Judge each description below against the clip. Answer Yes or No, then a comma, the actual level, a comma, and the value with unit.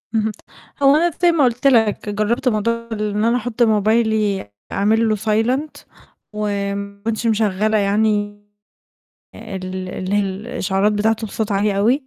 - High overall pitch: Yes, high, 215 Hz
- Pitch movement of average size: No, narrow, 2.1 semitones